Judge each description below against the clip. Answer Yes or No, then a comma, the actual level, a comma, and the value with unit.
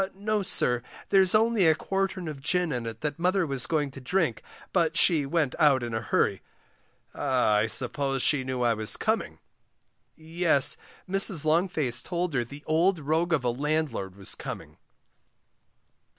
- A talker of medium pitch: Yes, medium, 150 Hz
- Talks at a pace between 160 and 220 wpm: Yes, average, 165 wpm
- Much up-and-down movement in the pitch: Yes, wide, 5.8 semitones